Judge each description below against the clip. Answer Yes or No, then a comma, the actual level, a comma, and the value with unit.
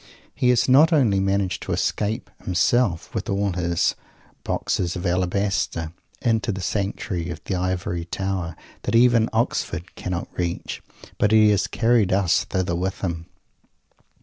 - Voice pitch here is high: No, very low, 95 Hz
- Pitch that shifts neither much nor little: Yes, average, 3.5 semitones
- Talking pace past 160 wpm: No, average, 145 wpm